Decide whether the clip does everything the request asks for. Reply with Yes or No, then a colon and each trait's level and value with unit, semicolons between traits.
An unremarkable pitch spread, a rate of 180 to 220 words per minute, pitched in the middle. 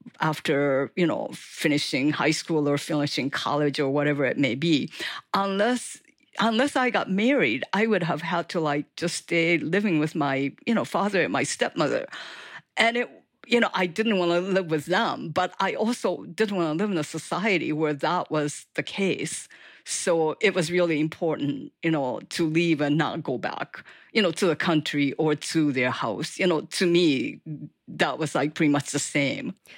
Yes: average, 4.6 semitones; average, 190 wpm; medium, 165 Hz